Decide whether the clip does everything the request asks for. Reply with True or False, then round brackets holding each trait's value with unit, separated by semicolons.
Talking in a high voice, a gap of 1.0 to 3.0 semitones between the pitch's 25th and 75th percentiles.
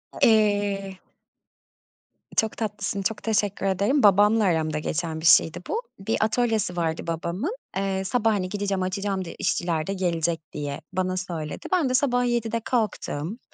False (195 Hz; 4.1 semitones)